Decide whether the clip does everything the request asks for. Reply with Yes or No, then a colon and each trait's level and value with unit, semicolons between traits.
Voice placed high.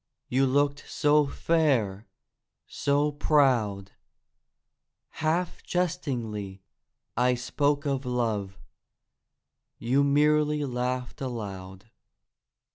No: low, 130 Hz